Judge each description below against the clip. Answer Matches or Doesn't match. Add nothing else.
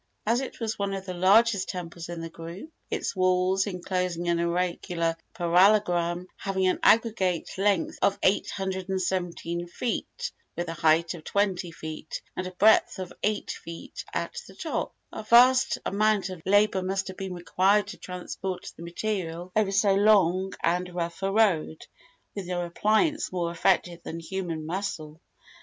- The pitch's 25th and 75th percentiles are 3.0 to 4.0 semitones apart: Doesn't match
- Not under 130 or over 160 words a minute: Matches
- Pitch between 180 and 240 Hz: Matches